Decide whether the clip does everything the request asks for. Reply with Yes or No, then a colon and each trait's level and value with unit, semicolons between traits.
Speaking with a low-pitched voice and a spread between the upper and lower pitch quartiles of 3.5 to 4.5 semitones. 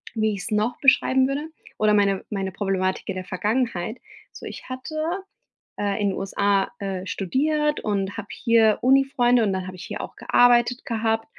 No: high, 215 Hz; average, 4.2 semitones